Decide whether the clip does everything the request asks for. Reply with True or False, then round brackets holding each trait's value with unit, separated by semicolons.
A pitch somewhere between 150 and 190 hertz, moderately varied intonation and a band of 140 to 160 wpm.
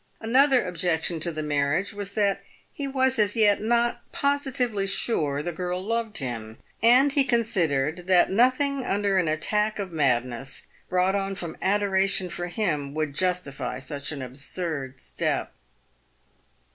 False (185 Hz; 6.2 semitones; 155 wpm)